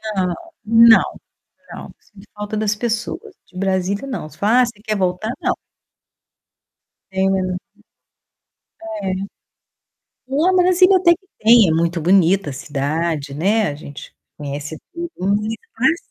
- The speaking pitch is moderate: No, high, 200 Hz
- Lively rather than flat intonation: Yes, wide, 5.8 semitones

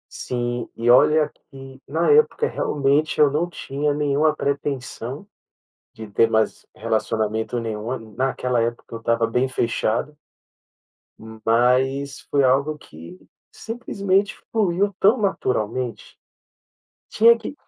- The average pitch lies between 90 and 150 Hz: Yes, low, 135 Hz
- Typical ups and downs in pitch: Yes, average, 4.9 semitones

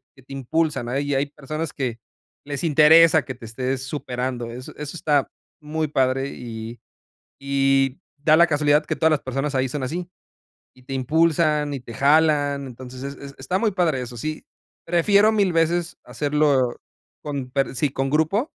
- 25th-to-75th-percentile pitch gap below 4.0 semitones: Yes, average, 3.1 semitones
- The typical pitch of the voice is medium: Yes, medium, 145 Hz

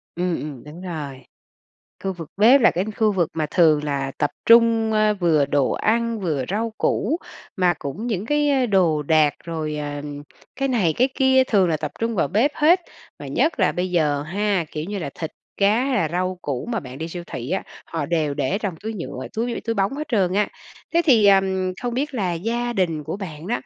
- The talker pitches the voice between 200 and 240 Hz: No, high, 190 Hz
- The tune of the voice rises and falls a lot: Yes, wide, 6.4 semitones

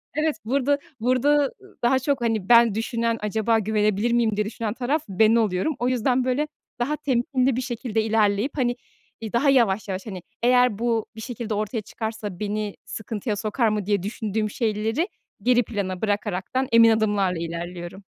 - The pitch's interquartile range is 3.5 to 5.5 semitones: No, average, 3.1 semitones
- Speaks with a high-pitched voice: Yes, high, 225 Hz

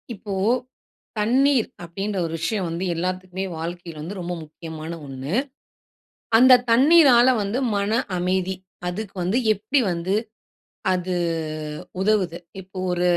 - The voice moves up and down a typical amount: Yes, average, 3.8 semitones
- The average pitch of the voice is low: No, medium, 185 Hz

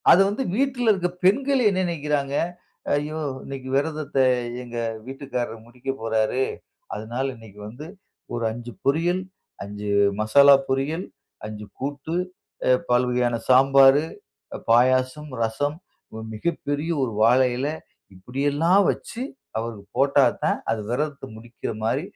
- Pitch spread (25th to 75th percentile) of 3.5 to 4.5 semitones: Yes, average, 4.2 semitones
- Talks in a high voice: No, low, 135 Hz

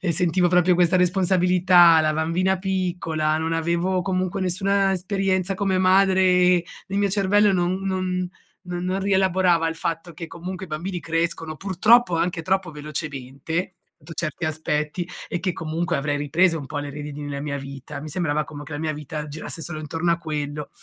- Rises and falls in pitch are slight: No, average, 3.1 semitones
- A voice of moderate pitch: Yes, medium, 175 Hz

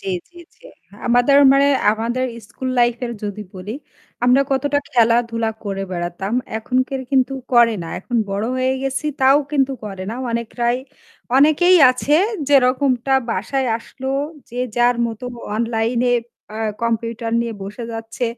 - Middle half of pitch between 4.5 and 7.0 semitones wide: No, average, 2.8 semitones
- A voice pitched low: No, high, 240 Hz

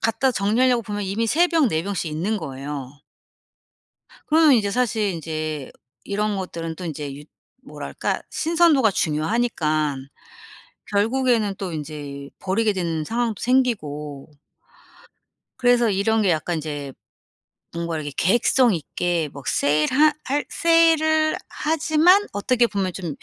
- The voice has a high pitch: Yes, high, 200 Hz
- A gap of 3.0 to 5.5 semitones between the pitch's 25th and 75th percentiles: No, wide, 8.0 semitones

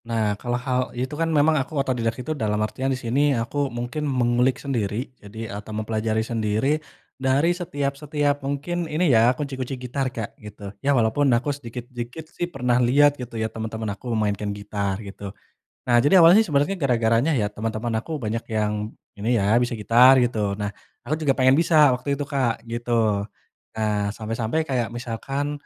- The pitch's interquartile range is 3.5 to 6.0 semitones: Yes, average, 4.1 semitones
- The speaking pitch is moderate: No, low, 120 Hz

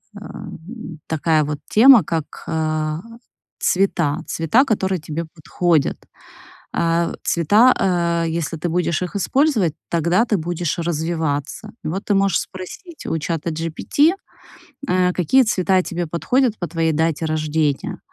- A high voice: No, medium, 170 Hz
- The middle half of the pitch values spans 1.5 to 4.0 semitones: Yes, average, 3.2 semitones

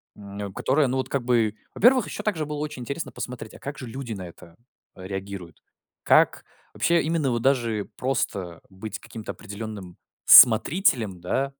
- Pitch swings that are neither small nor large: No, wide, 5.7 semitones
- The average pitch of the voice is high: No, low, 115 Hz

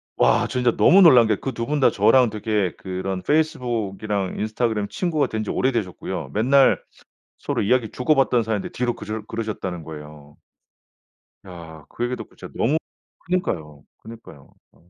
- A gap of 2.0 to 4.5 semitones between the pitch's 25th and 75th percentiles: No, average, 5.2 semitones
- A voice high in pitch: No, low, 110 Hz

